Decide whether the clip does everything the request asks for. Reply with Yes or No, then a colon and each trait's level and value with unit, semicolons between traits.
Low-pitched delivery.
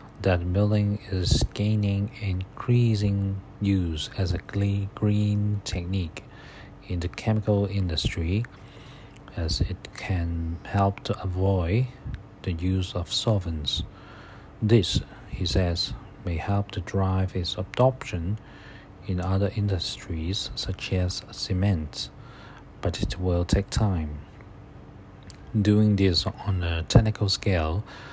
Yes: low, 100 Hz